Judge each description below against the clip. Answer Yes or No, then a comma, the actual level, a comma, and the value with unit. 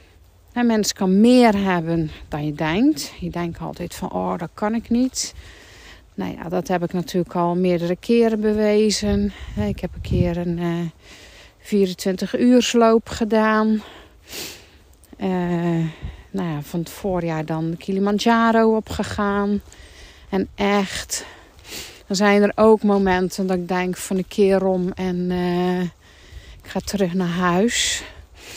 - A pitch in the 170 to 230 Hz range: Yes, medium, 185 Hz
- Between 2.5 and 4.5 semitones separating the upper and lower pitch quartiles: Yes, average, 3.8 semitones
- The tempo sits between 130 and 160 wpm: Yes, average, 140 wpm